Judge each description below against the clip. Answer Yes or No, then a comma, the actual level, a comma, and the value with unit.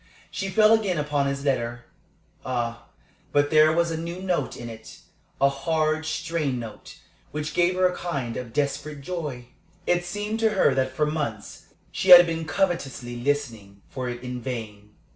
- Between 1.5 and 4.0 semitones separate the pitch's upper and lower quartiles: No, wide, 5.6 semitones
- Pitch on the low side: No, medium, 145 Hz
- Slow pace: No, average, 170 wpm